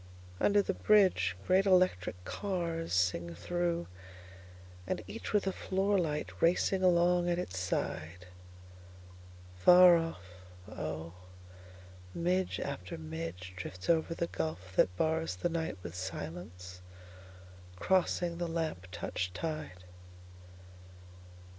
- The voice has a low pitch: Yes, very low, 95 Hz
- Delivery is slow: Yes, slow, 95 wpm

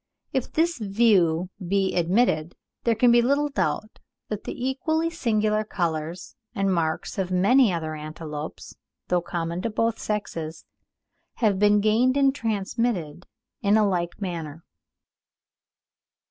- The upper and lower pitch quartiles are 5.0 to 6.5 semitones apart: Yes, average, 5.3 semitones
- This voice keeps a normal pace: No, slow, 130 wpm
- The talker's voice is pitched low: No, high, 200 Hz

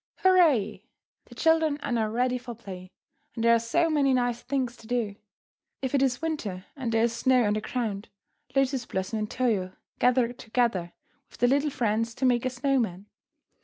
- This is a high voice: Yes, high, 240 Hz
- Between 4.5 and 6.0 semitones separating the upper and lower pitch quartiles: No, average, 3.2 semitones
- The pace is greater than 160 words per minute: Yes, average, 190 wpm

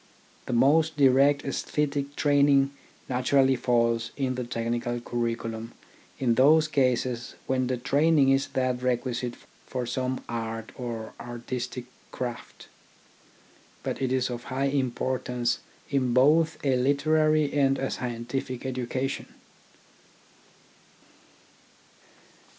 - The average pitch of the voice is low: Yes, low, 130 Hz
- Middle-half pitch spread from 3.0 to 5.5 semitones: No, narrow, 2.4 semitones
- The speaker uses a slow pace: Yes, slow, 105 wpm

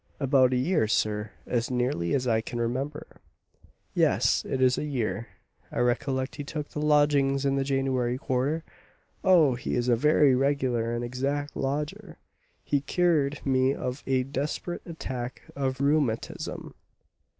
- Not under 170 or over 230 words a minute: No, average, 150 wpm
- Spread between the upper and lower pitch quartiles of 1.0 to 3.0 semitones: Yes, average, 2.7 semitones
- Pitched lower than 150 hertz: Yes, low, 135 Hz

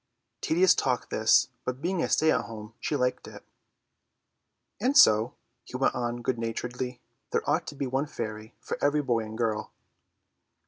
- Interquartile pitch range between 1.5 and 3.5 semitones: No, average, 3.9 semitones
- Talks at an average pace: Yes, average, 170 wpm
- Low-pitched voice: Yes, low, 125 Hz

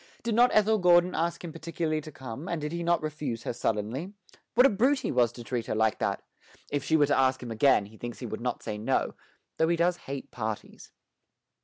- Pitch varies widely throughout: Yes, wide, 6.2 semitones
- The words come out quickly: Yes, fast, 230 wpm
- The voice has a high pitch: No, medium, 145 Hz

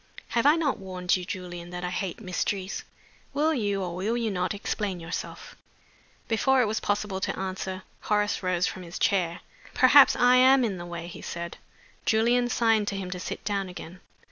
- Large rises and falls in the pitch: No, average, 3.8 semitones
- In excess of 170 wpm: Yes, average, 190 wpm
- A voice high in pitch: Yes, high, 195 Hz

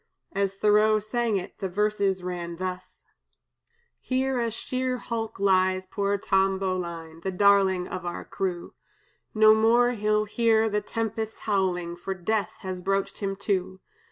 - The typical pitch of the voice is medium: No, high, 200 Hz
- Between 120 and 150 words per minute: Yes, average, 145 wpm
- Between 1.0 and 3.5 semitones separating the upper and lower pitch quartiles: Yes, average, 2.7 semitones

